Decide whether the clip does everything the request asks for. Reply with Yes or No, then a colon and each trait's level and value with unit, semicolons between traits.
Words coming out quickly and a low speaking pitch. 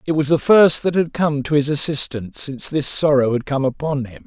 No: fast, 240 wpm; medium, 145 Hz